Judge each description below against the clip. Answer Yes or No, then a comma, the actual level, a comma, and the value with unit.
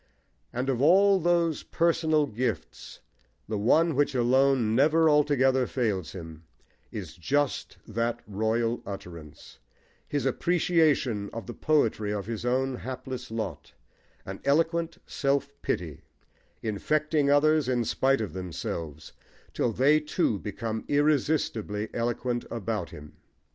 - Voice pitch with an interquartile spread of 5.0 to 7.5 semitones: Yes, wide, 5.4 semitones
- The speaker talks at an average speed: No, slow, 120 wpm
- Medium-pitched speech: No, low, 125 Hz